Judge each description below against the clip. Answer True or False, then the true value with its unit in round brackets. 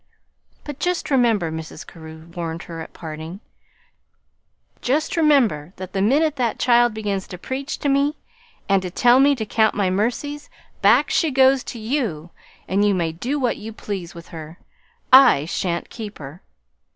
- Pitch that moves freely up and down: True (7.6 semitones)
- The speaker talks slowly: False (165 wpm)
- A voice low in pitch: False (210 Hz)